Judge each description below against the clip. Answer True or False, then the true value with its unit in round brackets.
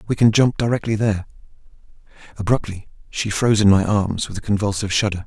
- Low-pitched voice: True (105 Hz)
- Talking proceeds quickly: False (170 wpm)